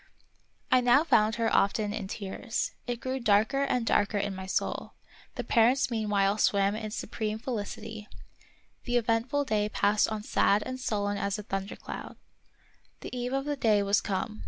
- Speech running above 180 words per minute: No, average, 165 wpm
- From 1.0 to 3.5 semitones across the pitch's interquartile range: Yes, average, 3.1 semitones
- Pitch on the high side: Yes, high, 215 Hz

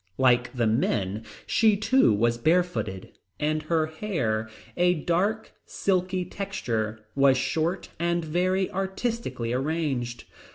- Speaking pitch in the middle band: Yes, medium, 155 Hz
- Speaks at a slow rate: Yes, slow, 120 wpm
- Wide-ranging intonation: Yes, wide, 7.4 semitones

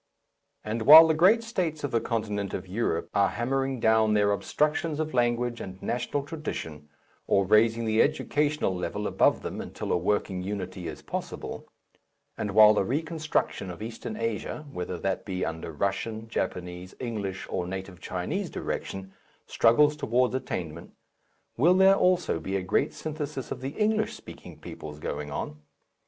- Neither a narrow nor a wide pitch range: No, wide, 7.3 semitones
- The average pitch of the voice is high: No, low, 110 Hz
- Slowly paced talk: No, average, 155 wpm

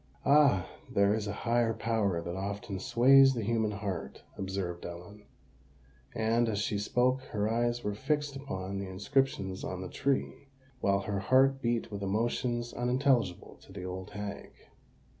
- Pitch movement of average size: Yes, average, 3.7 semitones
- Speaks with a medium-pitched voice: No, low, 105 Hz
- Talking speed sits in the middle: Yes, average, 155 wpm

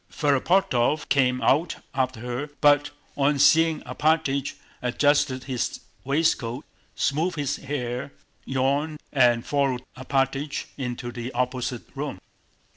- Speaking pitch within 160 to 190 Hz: No, low, 135 Hz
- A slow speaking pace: Yes, slow, 110 wpm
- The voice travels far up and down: No, narrow, 2.5 semitones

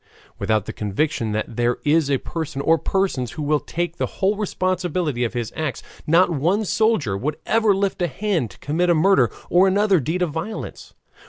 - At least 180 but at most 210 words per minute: Yes, average, 190 wpm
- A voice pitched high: No, medium, 160 Hz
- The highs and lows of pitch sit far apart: Yes, wide, 6.0 semitones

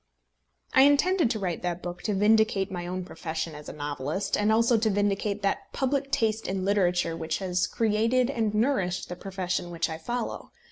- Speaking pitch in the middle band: No, high, 200 Hz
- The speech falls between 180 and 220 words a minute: Yes, average, 185 wpm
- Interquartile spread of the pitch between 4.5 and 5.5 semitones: No, average, 4.0 semitones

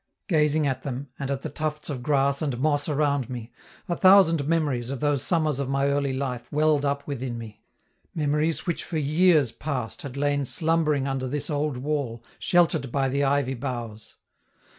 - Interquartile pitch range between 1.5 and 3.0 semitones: Yes, narrow, 2.4 semitones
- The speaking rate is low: No, average, 180 wpm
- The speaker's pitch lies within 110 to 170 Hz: Yes, medium, 140 Hz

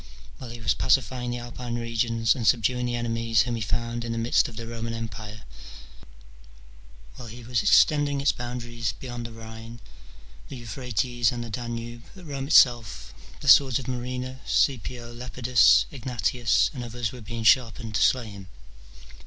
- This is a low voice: Yes, low, 120 Hz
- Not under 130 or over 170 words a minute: Yes, average, 165 wpm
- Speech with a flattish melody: Yes, narrow, 1.5 semitones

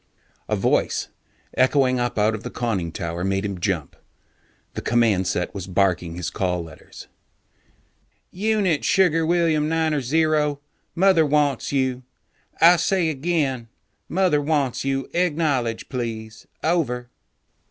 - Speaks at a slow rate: Yes, slow, 125 wpm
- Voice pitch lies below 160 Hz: Yes, low, 135 Hz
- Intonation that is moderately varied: No, wide, 7.0 semitones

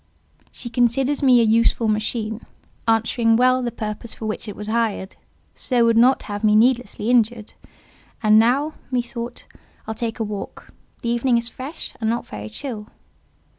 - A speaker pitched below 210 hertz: No, high, 230 Hz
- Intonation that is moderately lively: No, narrow, 2.2 semitones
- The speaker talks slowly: No, average, 165 wpm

